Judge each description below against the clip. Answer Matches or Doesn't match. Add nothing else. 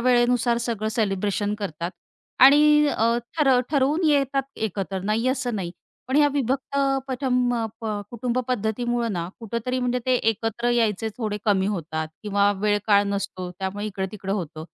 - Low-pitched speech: Doesn't match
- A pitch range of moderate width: Matches